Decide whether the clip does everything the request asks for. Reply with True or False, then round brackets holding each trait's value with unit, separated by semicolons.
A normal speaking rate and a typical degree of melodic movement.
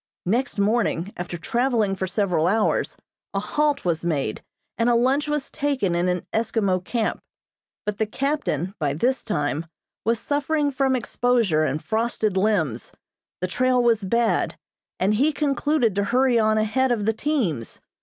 False (155 wpm; 5.8 semitones)